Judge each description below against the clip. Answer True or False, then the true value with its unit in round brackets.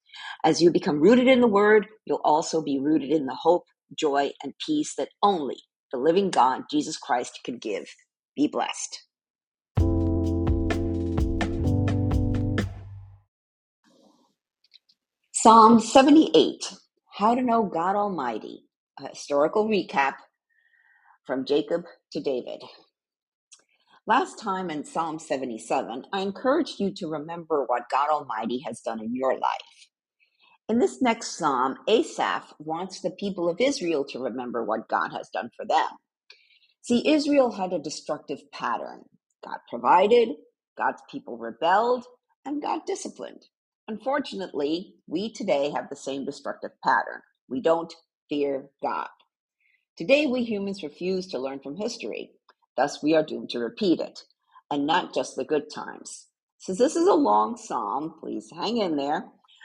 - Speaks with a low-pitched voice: False (190 Hz)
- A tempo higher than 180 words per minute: False (135 wpm)